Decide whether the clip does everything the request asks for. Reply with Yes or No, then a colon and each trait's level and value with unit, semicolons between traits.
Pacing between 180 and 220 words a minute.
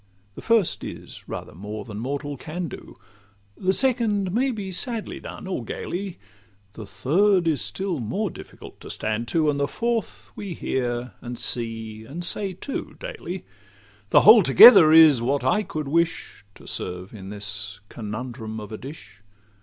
No: average, 160 wpm